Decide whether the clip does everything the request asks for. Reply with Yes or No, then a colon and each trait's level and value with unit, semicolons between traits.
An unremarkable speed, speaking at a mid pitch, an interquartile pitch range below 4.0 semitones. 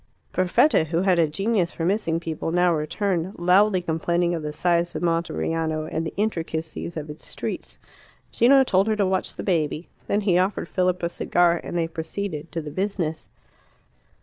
Yes: average, 175 wpm; medium, 175 Hz; average, 2.7 semitones